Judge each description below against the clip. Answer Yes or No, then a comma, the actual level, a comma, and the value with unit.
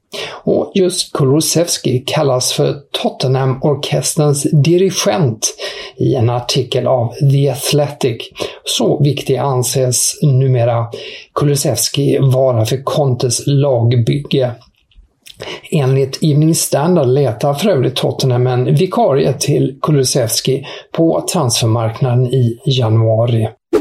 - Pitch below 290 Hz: Yes, low, 135 Hz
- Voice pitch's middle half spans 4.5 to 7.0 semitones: No, average, 2.7 semitones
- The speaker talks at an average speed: No, slow, 95 wpm